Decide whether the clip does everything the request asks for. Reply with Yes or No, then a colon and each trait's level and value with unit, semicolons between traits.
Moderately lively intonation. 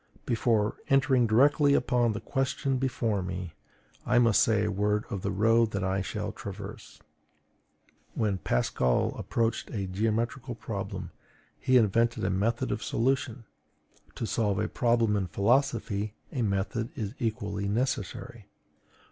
Yes: average, 3.3 semitones